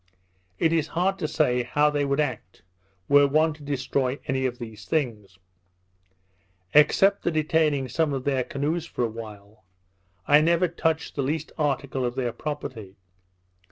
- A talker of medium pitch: Yes, medium, 145 Hz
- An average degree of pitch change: Yes, average, 3.9 semitones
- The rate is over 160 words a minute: No, average, 155 wpm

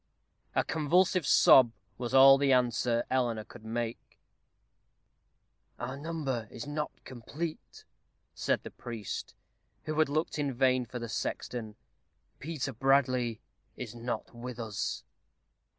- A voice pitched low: Yes, low, 125 Hz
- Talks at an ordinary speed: No, slow, 120 wpm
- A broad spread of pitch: No, average, 3.2 semitones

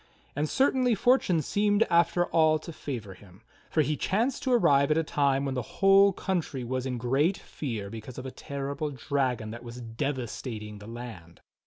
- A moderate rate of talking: Yes, average, 180 wpm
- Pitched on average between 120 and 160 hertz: Yes, medium, 140 Hz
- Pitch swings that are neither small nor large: No, wide, 6.1 semitones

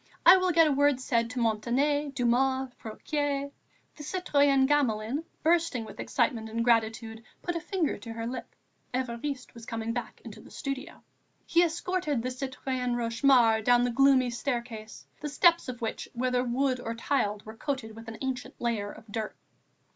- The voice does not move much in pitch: No, average, 3.7 semitones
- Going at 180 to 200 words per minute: No, average, 170 wpm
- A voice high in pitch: Yes, very high, 255 Hz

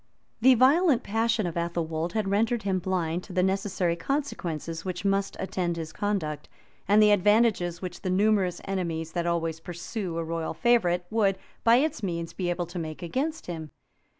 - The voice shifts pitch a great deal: No, average, 4.0 semitones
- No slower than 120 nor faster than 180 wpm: Yes, average, 175 wpm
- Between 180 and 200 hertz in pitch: Yes, medium, 185 Hz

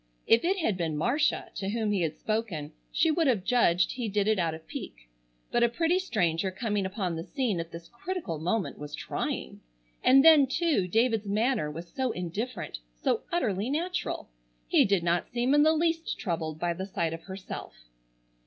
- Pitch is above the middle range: Yes, high, 205 Hz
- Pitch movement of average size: No, wide, 7.2 semitones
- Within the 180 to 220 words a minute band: Yes, average, 190 wpm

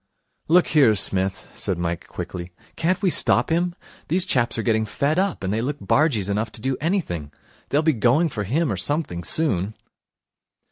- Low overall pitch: Yes, low, 125 Hz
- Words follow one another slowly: No, average, 180 wpm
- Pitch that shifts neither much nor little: No, wide, 8.4 semitones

